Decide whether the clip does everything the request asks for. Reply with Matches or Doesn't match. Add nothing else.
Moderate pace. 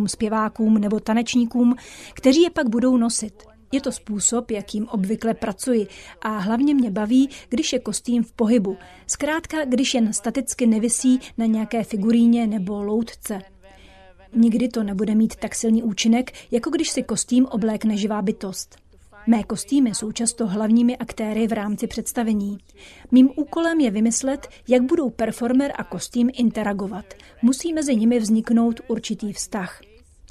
Matches